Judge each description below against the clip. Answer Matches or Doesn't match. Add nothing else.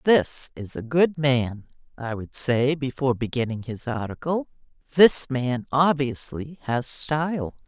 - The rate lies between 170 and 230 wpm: Doesn't match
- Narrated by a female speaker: Matches